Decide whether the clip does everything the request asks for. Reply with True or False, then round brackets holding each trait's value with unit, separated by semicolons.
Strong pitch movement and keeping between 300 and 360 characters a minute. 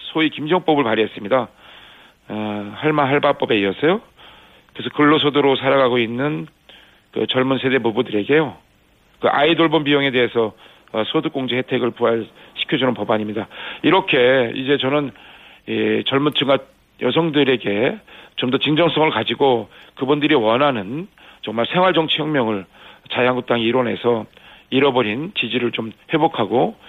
False (4.4 semitones; 315 characters per minute)